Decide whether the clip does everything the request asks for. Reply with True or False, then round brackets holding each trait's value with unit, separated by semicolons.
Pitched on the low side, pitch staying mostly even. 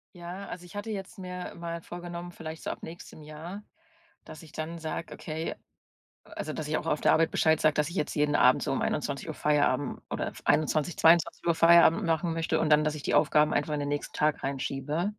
False (160 Hz; 2.3 semitones)